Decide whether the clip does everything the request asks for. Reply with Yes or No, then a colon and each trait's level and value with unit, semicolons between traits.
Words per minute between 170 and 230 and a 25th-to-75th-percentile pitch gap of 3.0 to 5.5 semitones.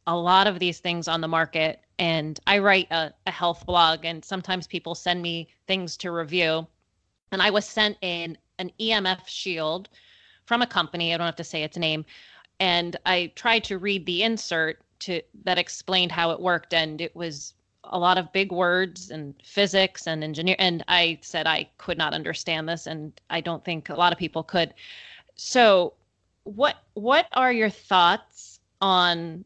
No: average, 185 wpm; narrow, 2.6 semitones